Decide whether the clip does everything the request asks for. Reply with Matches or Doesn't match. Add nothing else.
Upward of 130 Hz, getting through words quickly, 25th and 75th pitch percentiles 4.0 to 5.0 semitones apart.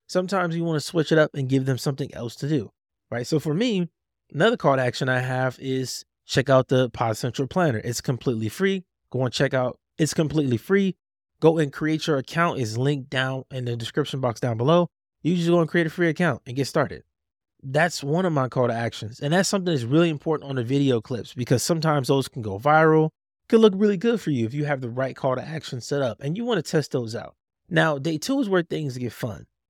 Matches